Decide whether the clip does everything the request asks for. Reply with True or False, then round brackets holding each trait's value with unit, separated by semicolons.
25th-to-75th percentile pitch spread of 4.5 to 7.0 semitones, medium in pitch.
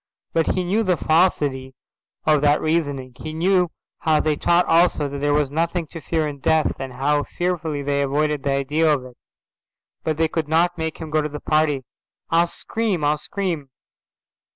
False (2.6 semitones; 155 Hz)